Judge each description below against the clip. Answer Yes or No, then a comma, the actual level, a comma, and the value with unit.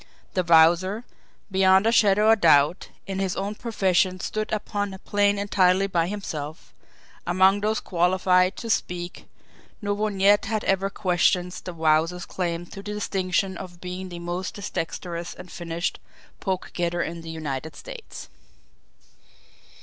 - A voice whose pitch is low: No, medium, 185 Hz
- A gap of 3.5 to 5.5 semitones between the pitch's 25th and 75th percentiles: No, narrow, 2.6 semitones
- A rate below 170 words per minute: Yes, average, 145 wpm